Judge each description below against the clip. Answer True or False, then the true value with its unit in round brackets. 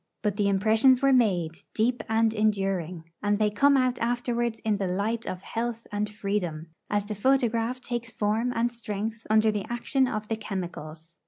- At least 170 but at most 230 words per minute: True (175 wpm)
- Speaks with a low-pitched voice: False (215 Hz)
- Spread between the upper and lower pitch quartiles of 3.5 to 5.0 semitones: False (3.0 semitones)